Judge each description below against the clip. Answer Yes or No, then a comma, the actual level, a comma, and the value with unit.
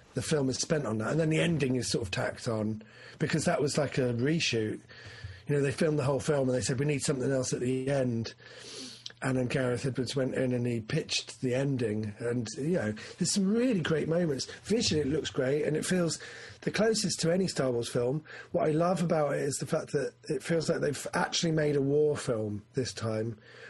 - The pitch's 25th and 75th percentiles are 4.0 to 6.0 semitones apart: Yes, average, 4.5 semitones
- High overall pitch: No, medium, 140 Hz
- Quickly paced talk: Yes, fast, 230 wpm